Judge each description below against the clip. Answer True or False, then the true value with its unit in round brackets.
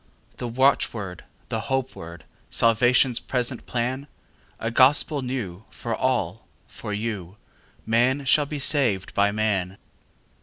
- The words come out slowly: True (100 wpm)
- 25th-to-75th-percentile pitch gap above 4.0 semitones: True (4.4 semitones)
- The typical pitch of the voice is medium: False (115 Hz)